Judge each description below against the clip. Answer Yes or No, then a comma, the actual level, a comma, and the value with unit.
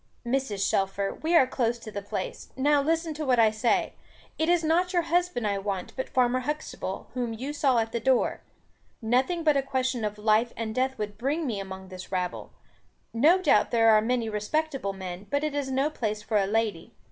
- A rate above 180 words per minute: Yes, fast, 205 wpm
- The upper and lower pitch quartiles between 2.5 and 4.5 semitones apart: No, average, 5.3 semitones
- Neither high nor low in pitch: No, high, 240 Hz